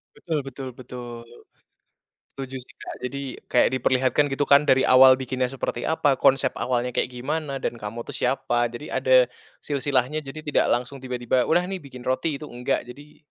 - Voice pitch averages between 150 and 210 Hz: No, low, 130 Hz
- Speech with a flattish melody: Yes, narrow, 2.1 semitones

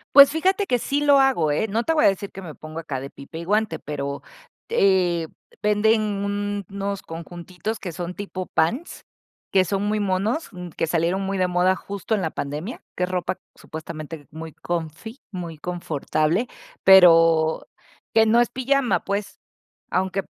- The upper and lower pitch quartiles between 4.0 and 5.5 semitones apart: Yes, average, 4.4 semitones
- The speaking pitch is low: No, high, 190 Hz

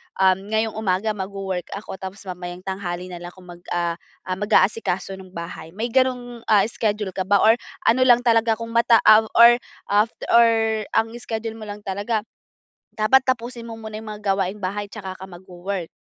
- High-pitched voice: Yes, high, 205 Hz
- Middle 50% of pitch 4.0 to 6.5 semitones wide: No, average, 3.1 semitones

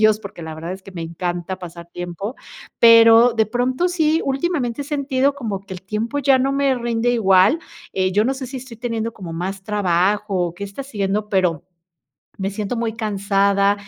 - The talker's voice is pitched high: Yes, high, 215 Hz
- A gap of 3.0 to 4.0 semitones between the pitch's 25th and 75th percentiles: No, average, 4.6 semitones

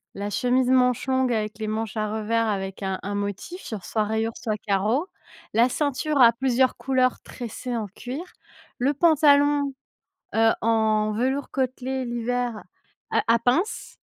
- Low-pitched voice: No, high, 240 Hz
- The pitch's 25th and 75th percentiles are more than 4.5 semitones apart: No, average, 3.3 semitones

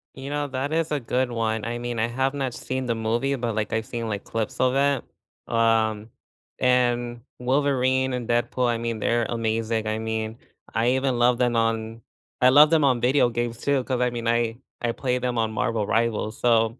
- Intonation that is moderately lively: No, narrow, 2.3 semitones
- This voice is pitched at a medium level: No, low, 120 Hz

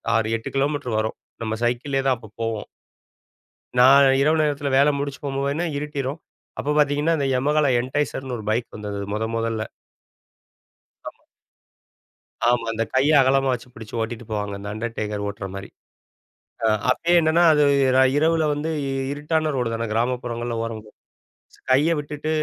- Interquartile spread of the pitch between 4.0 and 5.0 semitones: Yes, average, 4.3 semitones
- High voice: No, low, 130 Hz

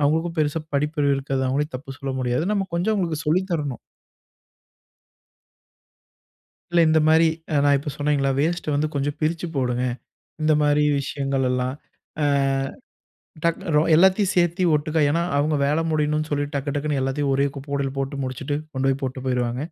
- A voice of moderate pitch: Yes, medium, 145 Hz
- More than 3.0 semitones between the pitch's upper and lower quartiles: No, narrow, 2.6 semitones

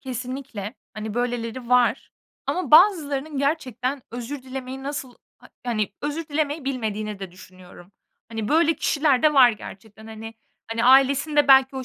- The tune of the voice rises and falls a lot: No, average, 4.2 semitones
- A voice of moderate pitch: No, very high, 255 Hz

